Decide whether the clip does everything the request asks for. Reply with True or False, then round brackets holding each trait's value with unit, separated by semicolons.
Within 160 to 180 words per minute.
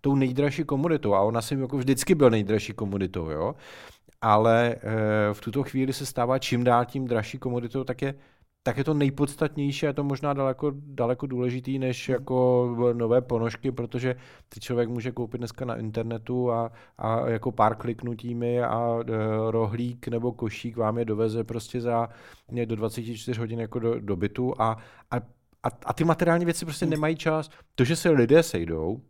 True (170 wpm)